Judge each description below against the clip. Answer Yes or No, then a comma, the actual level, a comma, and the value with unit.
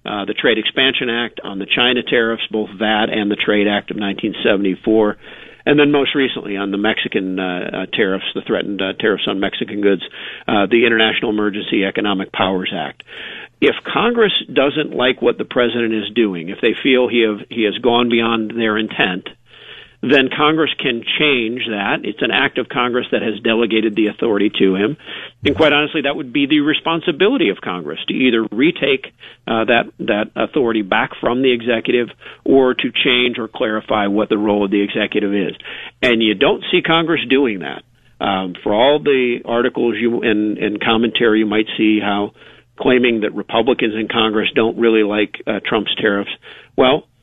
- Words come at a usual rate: Yes, average, 180 wpm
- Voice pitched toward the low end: Yes, low, 115 Hz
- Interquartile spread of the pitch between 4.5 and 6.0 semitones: No, average, 3.2 semitones